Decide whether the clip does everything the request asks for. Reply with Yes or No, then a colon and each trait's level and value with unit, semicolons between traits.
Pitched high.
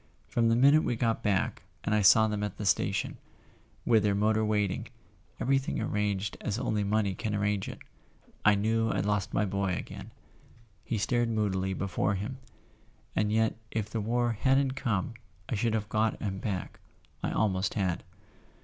No: low, 105 Hz